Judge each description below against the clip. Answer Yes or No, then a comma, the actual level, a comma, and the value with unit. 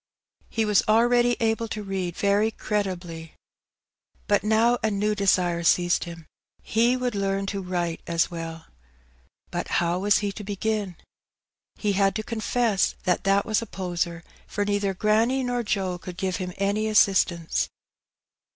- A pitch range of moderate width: Yes, average, 3.3 semitones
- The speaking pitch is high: Yes, high, 200 Hz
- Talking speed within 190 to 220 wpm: No, average, 155 wpm